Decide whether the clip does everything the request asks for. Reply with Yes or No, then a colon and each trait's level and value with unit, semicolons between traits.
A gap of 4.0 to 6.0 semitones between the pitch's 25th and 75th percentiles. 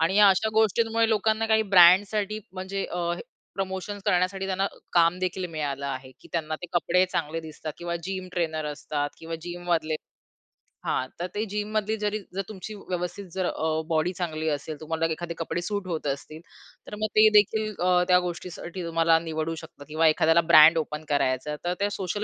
No: average, 3.6 semitones